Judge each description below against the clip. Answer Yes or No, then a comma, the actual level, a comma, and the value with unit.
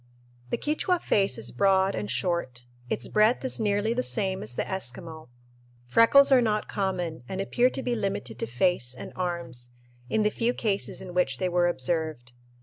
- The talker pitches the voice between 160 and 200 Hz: Yes, medium, 185 Hz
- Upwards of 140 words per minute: Yes, average, 180 wpm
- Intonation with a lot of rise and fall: Yes, wide, 8.7 semitones